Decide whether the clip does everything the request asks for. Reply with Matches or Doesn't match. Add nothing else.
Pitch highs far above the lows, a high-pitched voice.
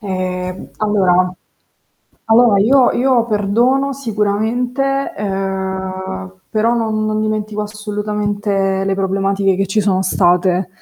Doesn't match